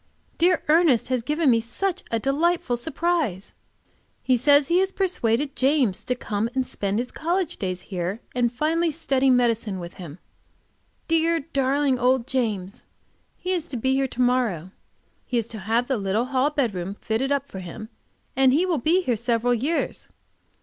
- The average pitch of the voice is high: Yes, very high, 255 Hz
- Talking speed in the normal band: Yes, average, 170 wpm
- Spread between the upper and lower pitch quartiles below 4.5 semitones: No, average, 5.1 semitones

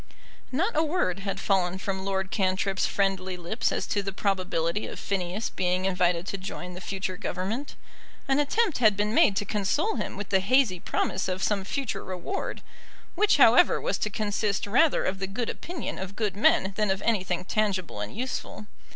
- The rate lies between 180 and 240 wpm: Yes, average, 185 wpm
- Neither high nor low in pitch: No, high, 195 Hz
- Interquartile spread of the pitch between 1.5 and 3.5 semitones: Yes, average, 2.7 semitones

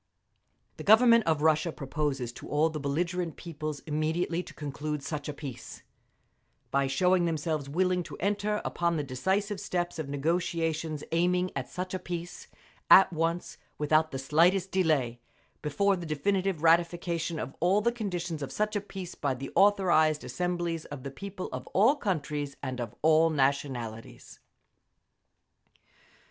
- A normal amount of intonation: Yes, average, 3.7 semitones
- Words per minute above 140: Yes, average, 150 wpm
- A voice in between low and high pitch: Yes, medium, 165 Hz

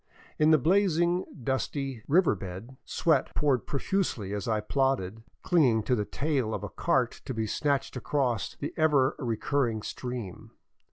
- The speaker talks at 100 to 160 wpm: Yes, average, 150 wpm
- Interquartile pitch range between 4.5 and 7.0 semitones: Yes, average, 5.2 semitones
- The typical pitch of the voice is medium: No, low, 130 Hz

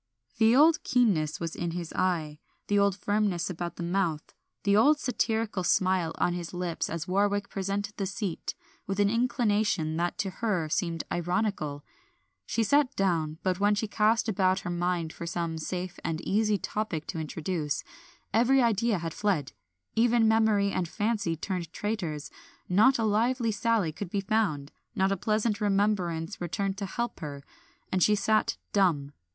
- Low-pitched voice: No, high, 195 Hz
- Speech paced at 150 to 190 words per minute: Yes, average, 165 wpm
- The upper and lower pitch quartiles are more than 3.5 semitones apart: Yes, average, 4.0 semitones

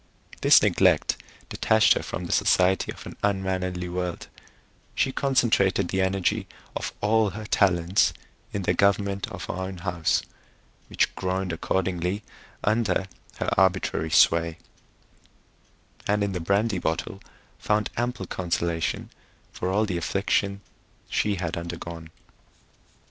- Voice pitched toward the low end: Yes, very low, 95 Hz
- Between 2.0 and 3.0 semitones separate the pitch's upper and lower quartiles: Yes, narrow, 2.6 semitones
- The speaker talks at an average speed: No, slow, 125 wpm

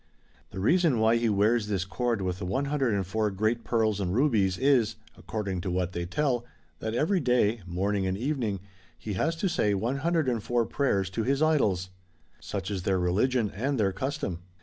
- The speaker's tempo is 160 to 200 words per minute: Yes, average, 170 wpm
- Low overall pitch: Yes, low, 110 Hz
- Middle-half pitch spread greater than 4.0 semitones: Yes, average, 5.2 semitones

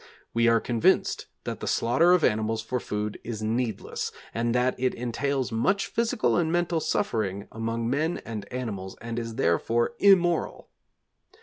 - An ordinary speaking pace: Yes, average, 150 wpm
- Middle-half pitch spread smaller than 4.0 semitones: No, average, 5.2 semitones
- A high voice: No, low, 115 Hz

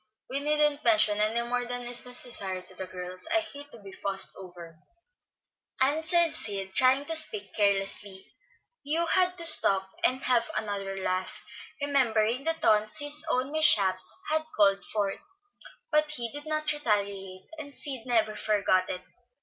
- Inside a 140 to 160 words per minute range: Yes, average, 155 wpm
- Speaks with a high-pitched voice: Yes, high, 230 Hz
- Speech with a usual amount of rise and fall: No, wide, 6.8 semitones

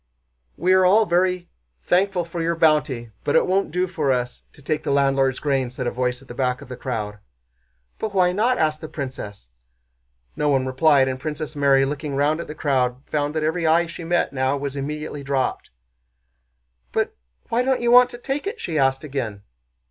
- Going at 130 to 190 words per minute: No, average, 200 wpm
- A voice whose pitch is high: No, medium, 150 Hz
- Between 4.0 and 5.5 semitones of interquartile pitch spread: Yes, average, 4.6 semitones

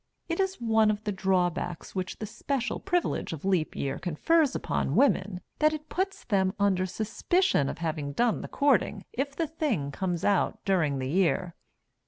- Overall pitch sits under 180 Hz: No, high, 200 Hz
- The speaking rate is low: No, average, 175 wpm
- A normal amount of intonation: No, wide, 8.0 semitones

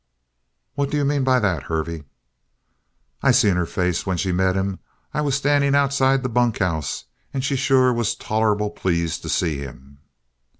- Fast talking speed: No, average, 170 wpm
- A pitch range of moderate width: No, wide, 7.3 semitones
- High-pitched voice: No, low, 105 Hz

